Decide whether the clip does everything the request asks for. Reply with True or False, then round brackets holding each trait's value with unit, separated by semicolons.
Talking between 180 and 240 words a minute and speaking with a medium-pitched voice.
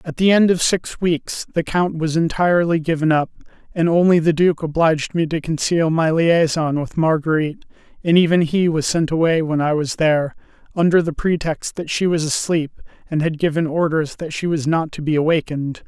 True (195 wpm; 160 Hz)